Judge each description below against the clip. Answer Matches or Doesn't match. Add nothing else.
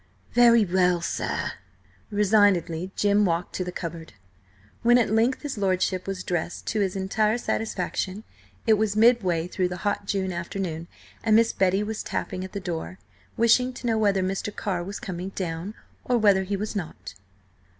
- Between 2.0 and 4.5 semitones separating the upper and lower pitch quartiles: Matches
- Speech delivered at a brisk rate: Doesn't match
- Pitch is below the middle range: Doesn't match